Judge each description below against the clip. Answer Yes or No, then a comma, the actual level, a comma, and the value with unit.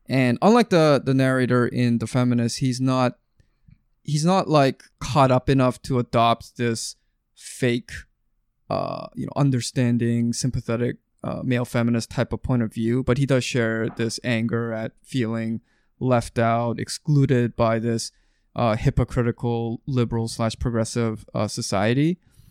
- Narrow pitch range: Yes, narrow, 2.0 semitones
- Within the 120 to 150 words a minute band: Yes, average, 140 wpm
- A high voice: No, low, 120 Hz